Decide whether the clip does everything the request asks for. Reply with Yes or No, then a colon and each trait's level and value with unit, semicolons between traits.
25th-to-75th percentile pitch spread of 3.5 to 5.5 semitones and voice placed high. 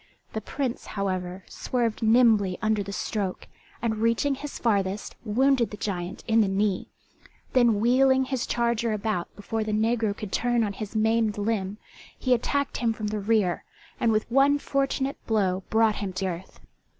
No: average, 2.9 semitones; high, 220 Hz